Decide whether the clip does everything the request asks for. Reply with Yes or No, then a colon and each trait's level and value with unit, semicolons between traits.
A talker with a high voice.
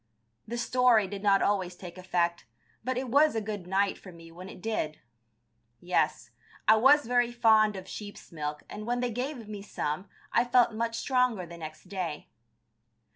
Yes: high, 210 Hz